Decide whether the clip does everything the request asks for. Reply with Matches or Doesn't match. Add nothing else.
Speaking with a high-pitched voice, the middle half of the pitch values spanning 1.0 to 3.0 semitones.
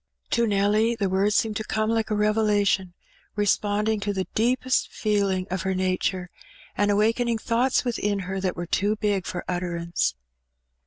Matches